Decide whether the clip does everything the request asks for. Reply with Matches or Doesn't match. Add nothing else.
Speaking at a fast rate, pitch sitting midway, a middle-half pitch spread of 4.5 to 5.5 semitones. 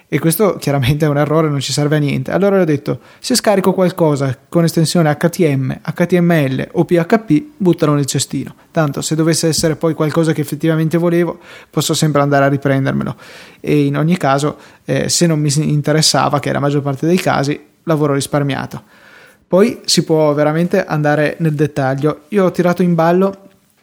Doesn't match